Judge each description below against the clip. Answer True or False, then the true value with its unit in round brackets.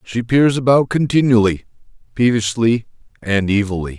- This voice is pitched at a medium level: False (115 Hz)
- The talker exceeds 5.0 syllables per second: False (4.9 syllables/s)